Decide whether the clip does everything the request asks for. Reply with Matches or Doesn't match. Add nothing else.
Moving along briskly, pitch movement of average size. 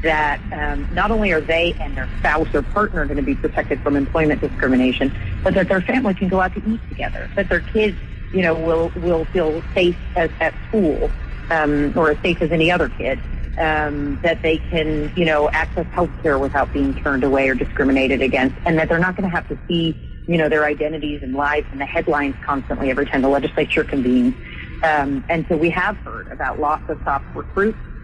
Matches